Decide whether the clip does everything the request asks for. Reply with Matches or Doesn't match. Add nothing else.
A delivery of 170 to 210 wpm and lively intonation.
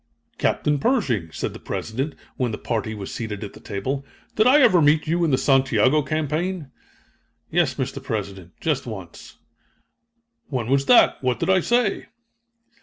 Doesn't match